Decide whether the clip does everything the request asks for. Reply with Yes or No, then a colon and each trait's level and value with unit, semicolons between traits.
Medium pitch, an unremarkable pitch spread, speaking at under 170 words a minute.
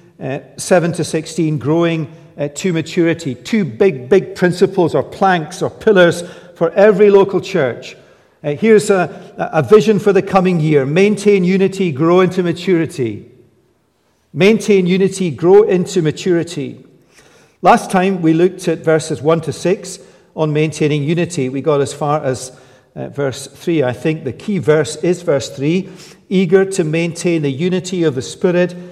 Yes: medium, 175 Hz; average, 3.4 semitones; average, 155 wpm